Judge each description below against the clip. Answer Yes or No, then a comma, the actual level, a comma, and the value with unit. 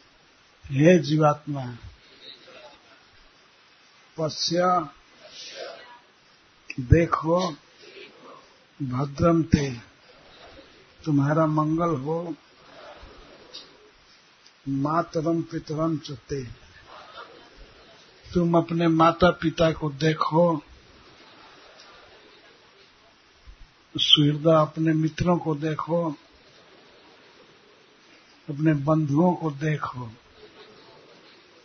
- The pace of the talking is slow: Yes, slow, 50 wpm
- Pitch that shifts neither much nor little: No, narrow, 2.2 semitones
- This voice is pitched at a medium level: Yes, medium, 160 Hz